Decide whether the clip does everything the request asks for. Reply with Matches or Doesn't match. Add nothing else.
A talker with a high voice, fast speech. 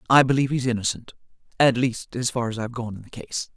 Doesn't match